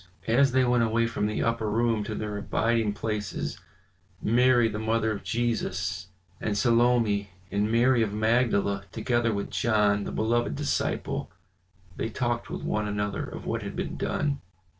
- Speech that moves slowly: No, average, 160 wpm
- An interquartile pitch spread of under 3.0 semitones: Yes, narrow, 2.4 semitones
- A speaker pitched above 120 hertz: No, low, 110 Hz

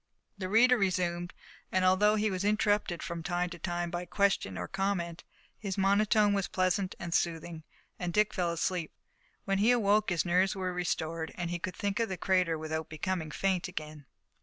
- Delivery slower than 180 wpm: No, average, 185 wpm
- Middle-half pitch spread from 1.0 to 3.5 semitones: Yes, average, 2.7 semitones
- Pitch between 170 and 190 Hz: Yes, medium, 185 Hz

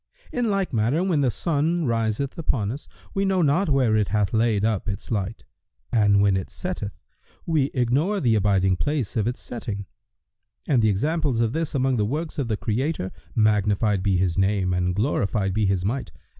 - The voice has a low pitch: Yes, low, 115 Hz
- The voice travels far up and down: Yes, wide, 6.1 semitones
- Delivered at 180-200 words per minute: Yes, average, 190 wpm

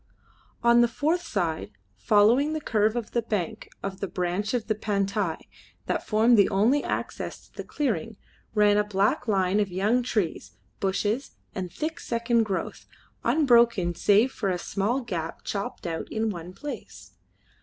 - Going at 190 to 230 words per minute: No, average, 160 wpm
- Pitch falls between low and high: No, high, 210 Hz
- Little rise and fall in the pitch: No, average, 3.6 semitones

